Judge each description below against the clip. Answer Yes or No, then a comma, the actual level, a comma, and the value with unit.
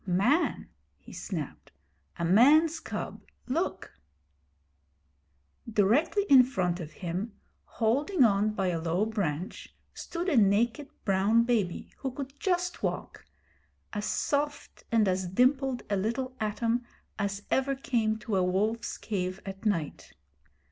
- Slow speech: Yes, slow, 125 wpm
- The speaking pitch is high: Yes, high, 220 Hz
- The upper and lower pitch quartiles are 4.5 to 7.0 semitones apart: Yes, wide, 5.6 semitones